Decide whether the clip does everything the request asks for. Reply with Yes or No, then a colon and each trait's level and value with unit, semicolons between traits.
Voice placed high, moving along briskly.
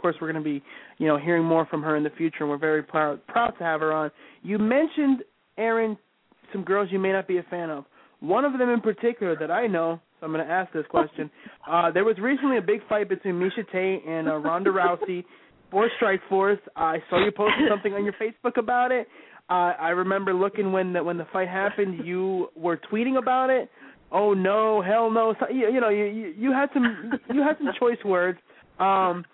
Yes: high, 195 Hz; fast, 225 wpm